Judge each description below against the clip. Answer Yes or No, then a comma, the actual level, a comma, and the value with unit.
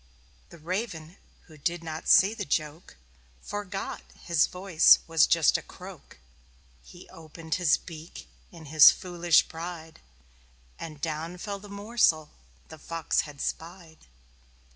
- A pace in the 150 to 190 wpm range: No, slow, 135 wpm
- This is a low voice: No, medium, 165 Hz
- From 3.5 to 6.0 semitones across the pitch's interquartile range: No, narrow, 2.4 semitones